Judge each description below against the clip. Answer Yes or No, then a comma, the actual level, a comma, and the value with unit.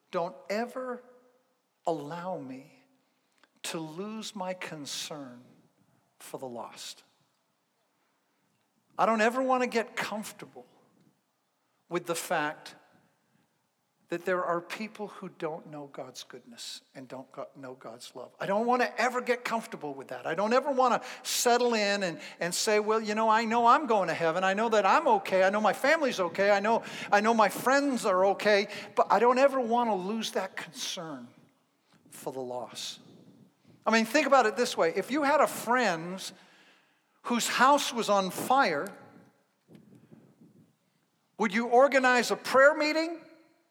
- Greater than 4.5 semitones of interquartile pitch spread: Yes, wide, 5.4 semitones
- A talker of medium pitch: No, high, 215 Hz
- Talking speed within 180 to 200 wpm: No, average, 155 wpm